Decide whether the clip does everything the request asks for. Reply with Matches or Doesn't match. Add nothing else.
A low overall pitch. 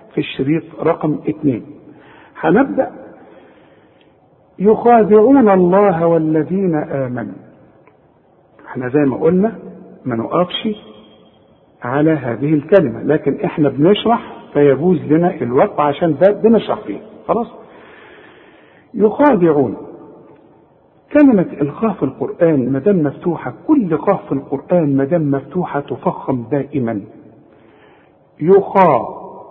Doesn't match